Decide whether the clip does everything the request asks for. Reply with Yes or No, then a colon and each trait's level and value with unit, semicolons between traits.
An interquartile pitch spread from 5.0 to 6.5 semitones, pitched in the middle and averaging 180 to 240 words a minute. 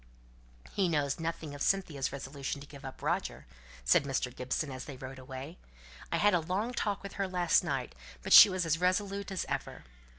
Yes: wide, 5.6 semitones; medium, 160 Hz; average, 195 wpm